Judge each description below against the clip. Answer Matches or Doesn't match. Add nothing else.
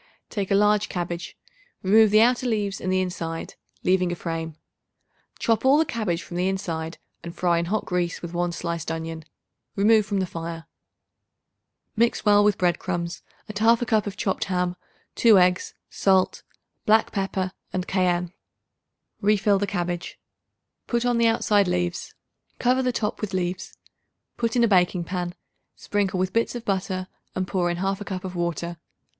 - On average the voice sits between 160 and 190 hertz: Matches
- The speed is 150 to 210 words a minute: Matches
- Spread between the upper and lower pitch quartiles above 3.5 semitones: Doesn't match